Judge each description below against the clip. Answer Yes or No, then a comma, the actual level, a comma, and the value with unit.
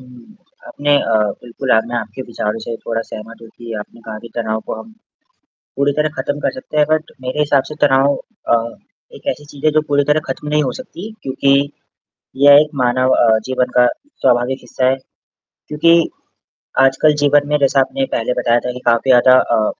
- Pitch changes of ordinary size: Yes, average, 3.7 semitones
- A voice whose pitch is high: No, low, 130 Hz